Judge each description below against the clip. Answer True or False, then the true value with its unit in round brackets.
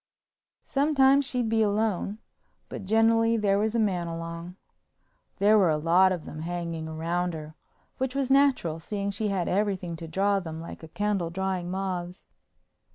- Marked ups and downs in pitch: False (4.4 semitones)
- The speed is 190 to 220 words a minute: False (160 wpm)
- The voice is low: False (190 Hz)